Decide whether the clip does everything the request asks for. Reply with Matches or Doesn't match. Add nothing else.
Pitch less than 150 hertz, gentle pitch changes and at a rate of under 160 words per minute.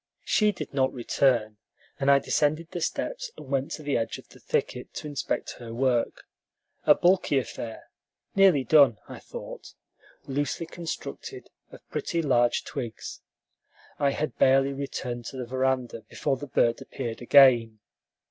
Doesn't match